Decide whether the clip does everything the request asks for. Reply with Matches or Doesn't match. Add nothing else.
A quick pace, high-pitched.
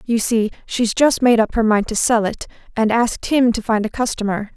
Matches